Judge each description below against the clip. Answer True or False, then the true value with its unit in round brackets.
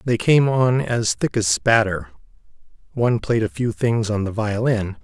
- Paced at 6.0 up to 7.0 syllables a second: False (4.5 syllables/s)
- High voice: False (115 Hz)